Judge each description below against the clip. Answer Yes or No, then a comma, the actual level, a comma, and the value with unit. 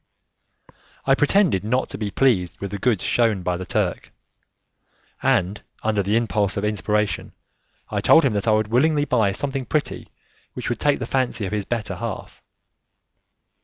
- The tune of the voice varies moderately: Yes, average, 4.4 semitones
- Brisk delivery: No, average, 165 wpm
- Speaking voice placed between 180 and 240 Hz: No, low, 110 Hz